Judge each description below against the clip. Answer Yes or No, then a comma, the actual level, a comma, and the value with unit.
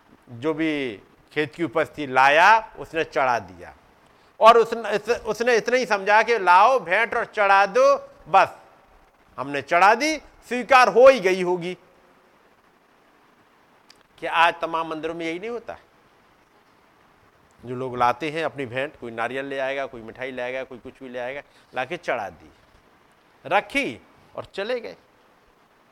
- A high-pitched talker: No, medium, 165 Hz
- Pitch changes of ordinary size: No, wide, 9.0 semitones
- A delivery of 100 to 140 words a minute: No, average, 150 wpm